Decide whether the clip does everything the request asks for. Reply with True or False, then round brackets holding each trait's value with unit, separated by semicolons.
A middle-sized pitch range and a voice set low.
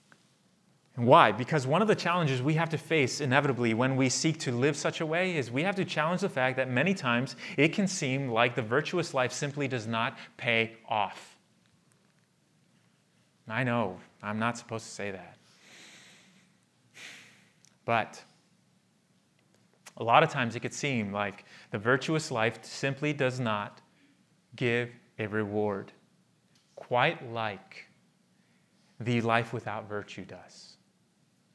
True (5.0 semitones; 130 Hz)